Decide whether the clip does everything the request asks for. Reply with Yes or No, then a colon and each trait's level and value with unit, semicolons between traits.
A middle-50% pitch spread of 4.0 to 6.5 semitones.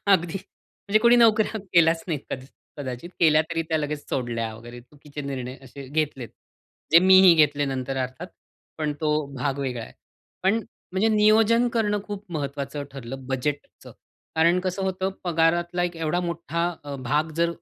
Yes: average, 5.0 semitones